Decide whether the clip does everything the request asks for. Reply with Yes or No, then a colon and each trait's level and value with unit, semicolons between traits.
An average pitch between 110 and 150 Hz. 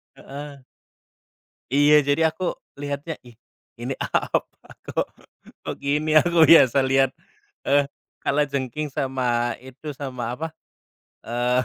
Yes: medium, 140 Hz